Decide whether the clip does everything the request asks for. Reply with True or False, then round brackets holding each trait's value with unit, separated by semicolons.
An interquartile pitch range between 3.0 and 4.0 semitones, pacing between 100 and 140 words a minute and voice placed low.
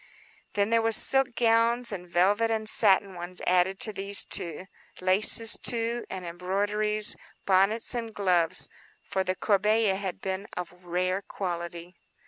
False (3.4 semitones; 135 wpm; 200 Hz)